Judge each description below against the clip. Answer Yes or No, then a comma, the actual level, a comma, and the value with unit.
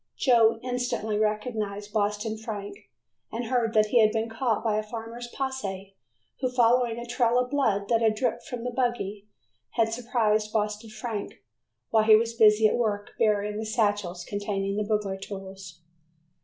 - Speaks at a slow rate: No, average, 165 wpm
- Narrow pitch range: Yes, narrow, 2.2 semitones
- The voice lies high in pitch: Yes, high, 220 Hz